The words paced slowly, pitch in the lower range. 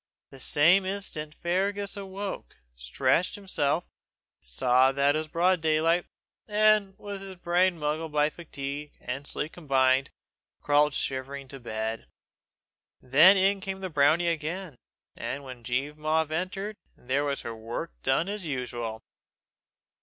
No: slow, 130 wpm; medium, 155 Hz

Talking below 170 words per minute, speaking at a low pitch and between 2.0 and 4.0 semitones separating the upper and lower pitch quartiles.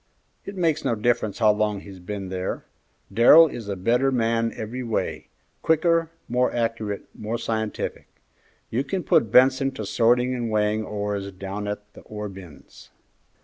Yes: average, 155 wpm; low, 110 Hz; average, 3.2 semitones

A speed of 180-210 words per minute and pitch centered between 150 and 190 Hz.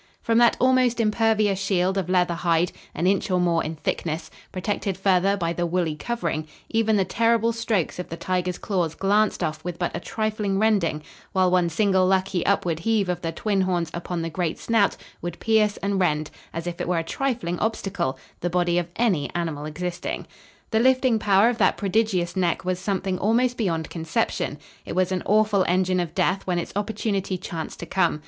Yes: average, 195 wpm; medium, 185 Hz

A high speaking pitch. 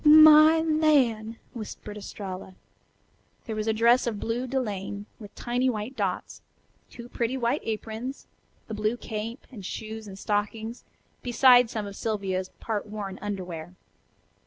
Yes: high, 220 Hz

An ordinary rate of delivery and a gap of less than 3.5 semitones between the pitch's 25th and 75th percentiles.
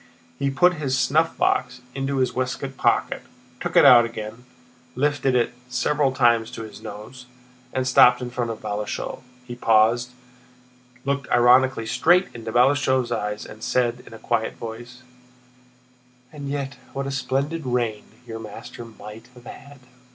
Yes: average, 150 wpm; average, 2.8 semitones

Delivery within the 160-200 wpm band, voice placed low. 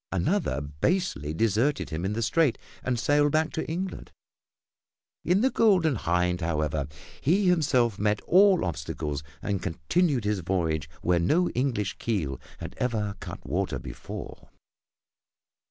No: slow, 135 wpm; low, 105 Hz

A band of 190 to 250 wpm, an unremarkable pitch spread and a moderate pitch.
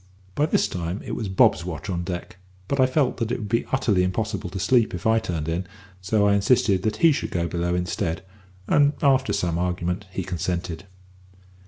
No: average, 200 wpm; average, 4.4 semitones; very low, 95 Hz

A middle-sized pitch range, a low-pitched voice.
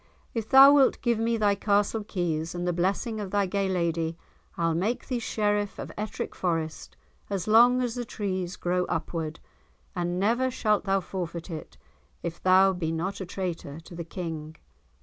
No: average, 3.9 semitones; high, 190 Hz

